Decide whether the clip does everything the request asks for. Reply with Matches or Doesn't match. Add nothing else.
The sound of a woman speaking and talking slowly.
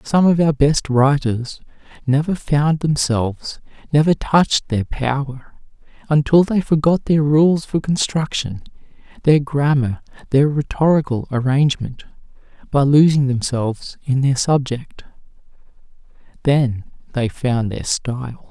Doesn't match